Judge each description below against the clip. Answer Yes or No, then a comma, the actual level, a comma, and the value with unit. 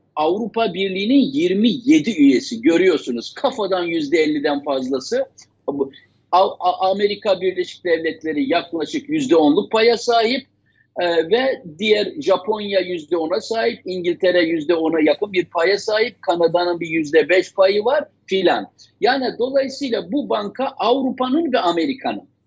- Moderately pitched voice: No, high, 200 Hz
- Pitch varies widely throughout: Yes, wide, 6.8 semitones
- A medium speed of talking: Yes, average, 115 wpm